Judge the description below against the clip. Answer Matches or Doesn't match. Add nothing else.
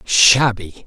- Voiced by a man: Matches